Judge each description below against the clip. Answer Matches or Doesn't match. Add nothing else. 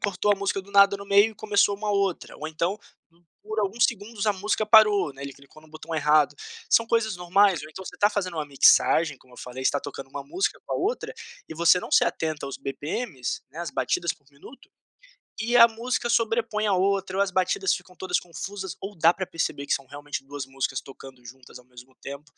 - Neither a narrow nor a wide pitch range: Doesn't match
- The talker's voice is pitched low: Doesn't match